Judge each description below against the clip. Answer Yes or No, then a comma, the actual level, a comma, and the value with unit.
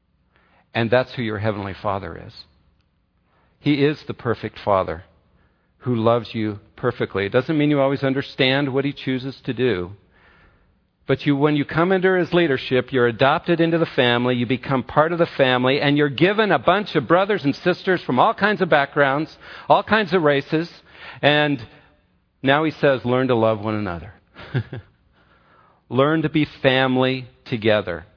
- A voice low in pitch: Yes, low, 130 Hz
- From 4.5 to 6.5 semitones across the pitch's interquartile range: Yes, wide, 5.4 semitones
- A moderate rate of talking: Yes, average, 165 wpm